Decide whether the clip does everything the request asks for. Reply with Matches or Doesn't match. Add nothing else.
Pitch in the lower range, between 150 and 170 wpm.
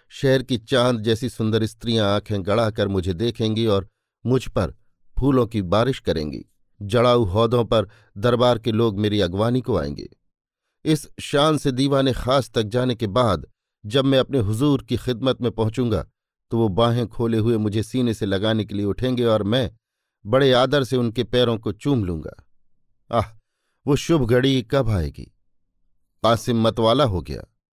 Matches